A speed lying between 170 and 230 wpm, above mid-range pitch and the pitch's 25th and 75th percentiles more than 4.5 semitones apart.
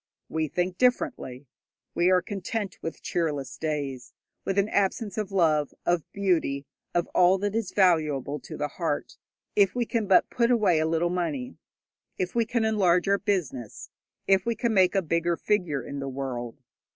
No: average, 175 wpm; medium, 180 Hz; average, 5.1 semitones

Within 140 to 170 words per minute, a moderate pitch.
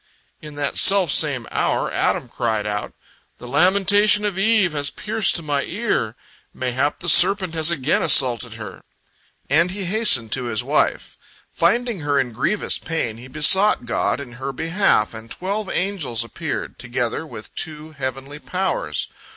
Yes: average, 155 wpm; medium, 150 Hz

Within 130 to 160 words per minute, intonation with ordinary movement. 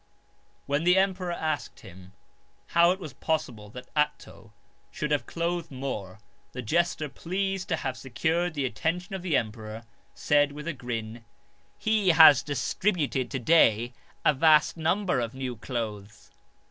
No: average, 145 wpm; wide, 5.8 semitones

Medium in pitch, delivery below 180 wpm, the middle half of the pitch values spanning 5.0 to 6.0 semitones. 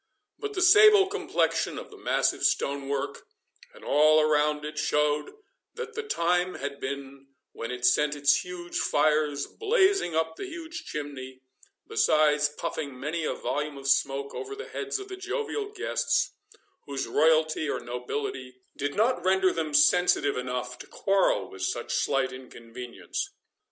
Yes: medium, 150 Hz; average, 150 wpm; wide, 5.6 semitones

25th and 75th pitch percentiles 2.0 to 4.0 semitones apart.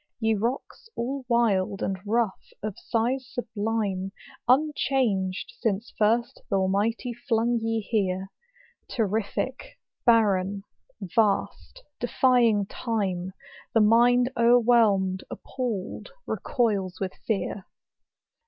Yes: average, 3.5 semitones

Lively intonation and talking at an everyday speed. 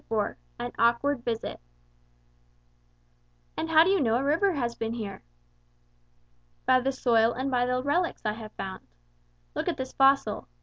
No: average, 3.5 semitones; average, 160 wpm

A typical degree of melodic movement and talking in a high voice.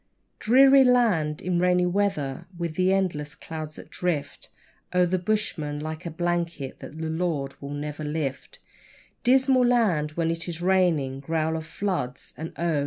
No: average, 3.5 semitones; medium, 165 Hz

